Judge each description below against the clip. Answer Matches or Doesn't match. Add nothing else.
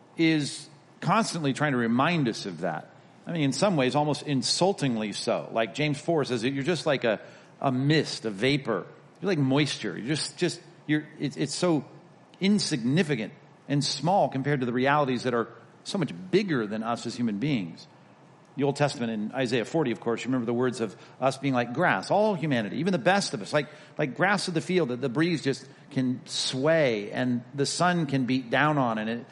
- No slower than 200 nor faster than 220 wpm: Matches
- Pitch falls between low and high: Matches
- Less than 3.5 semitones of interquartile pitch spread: Doesn't match